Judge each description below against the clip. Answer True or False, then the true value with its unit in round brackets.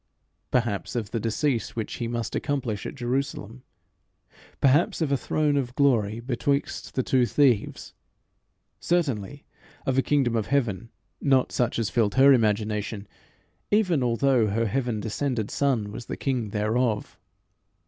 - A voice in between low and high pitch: False (120 Hz)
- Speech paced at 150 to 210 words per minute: False (140 wpm)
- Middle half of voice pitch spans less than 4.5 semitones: True (4.0 semitones)